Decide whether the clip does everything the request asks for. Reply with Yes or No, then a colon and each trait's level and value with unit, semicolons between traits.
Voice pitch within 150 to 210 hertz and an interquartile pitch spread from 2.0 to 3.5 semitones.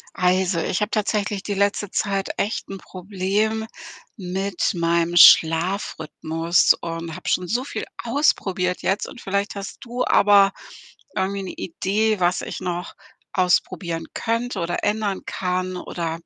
Yes: high, 190 Hz; average, 2.7 semitones